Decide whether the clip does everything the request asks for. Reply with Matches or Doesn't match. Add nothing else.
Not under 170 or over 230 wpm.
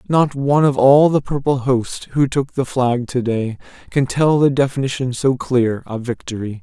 Matches